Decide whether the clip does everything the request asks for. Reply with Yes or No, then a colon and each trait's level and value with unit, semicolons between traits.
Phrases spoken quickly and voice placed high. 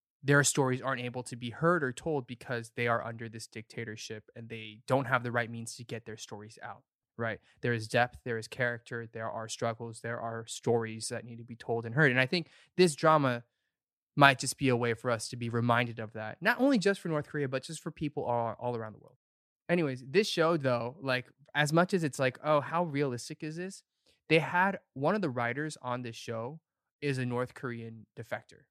No: fast, 225 wpm; low, 125 Hz